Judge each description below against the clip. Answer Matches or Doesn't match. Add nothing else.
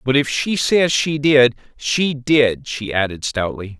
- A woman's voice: Doesn't match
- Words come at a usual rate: Matches